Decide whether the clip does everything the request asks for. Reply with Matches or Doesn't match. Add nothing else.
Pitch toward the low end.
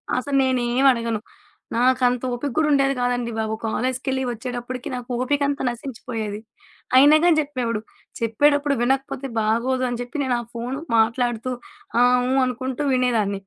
Doesn't match